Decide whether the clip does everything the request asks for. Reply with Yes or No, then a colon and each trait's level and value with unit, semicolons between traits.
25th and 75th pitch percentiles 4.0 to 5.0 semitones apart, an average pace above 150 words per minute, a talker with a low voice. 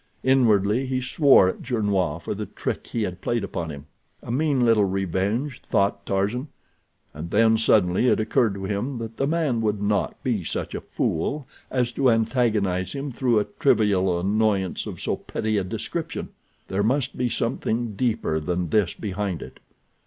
Yes: average, 4.3 semitones; average, 170 wpm; low, 110 Hz